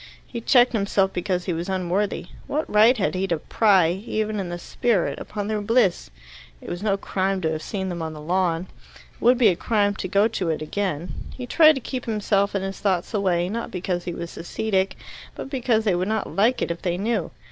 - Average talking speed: No, fast, 225 wpm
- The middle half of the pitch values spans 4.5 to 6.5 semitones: No, average, 3.6 semitones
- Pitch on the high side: Yes, high, 195 Hz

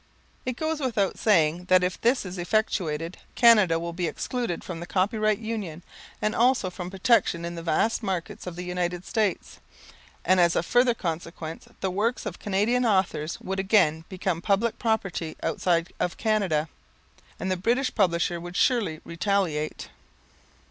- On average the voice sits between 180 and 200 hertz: Yes, medium, 185 Hz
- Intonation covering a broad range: No, average, 4.2 semitones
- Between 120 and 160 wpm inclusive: Yes, average, 155 wpm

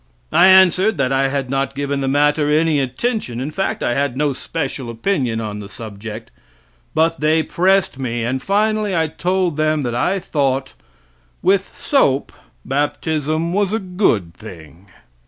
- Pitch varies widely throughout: Yes, wide, 5.9 semitones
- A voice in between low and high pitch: Yes, medium, 145 Hz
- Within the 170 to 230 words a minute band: No, average, 155 wpm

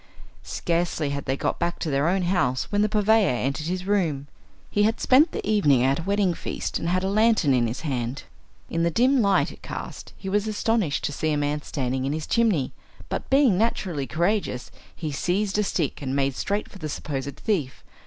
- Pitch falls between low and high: Yes, medium, 170 Hz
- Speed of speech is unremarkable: No, fast, 210 wpm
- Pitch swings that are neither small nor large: No, wide, 6.6 semitones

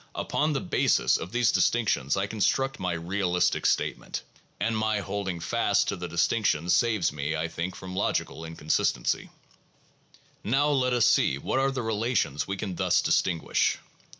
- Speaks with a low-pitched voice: Yes, low, 100 Hz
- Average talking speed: Yes, average, 160 wpm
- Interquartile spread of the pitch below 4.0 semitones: No, wide, 5.5 semitones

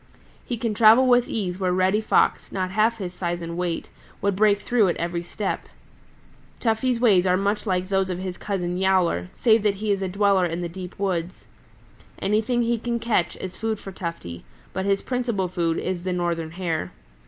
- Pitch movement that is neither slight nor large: Yes, average, 3.3 semitones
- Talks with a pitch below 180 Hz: No, high, 190 Hz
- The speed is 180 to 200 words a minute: Yes, average, 195 wpm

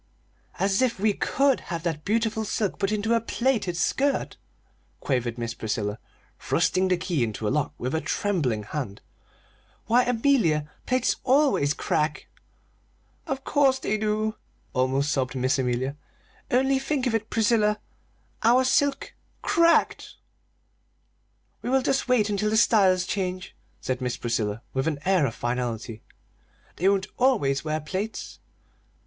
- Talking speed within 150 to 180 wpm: No, average, 140 wpm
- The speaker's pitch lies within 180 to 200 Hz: Yes, high, 190 Hz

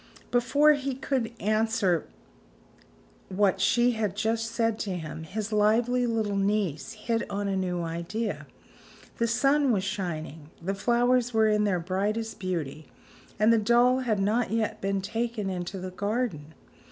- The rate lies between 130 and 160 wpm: Yes, average, 150 wpm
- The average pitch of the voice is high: Yes, high, 215 Hz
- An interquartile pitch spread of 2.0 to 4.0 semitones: Yes, average, 3.5 semitones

